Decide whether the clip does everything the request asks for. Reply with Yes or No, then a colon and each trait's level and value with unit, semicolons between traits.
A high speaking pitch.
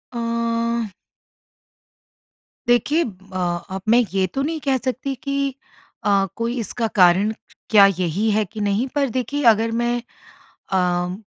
Yes: high, 230 Hz